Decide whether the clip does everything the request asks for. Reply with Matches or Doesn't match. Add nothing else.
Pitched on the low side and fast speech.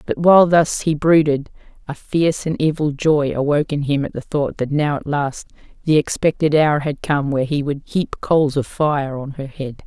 Doesn't match